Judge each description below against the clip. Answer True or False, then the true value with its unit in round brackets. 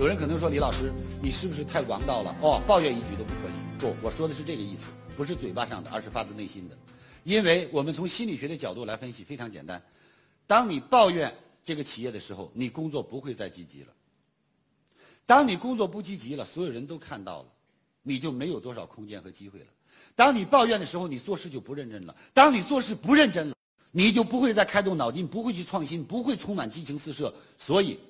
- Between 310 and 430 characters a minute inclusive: True (340 characters per minute)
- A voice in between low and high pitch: True (150 Hz)